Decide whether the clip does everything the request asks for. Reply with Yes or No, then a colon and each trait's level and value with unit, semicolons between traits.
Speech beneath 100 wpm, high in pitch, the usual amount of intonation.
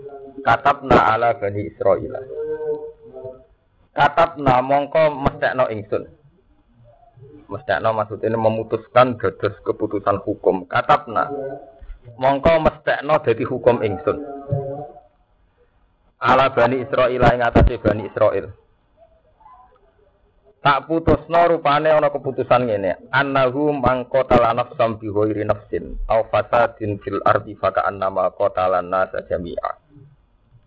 No: slow, 85 wpm; low, 135 Hz; average, 4.8 semitones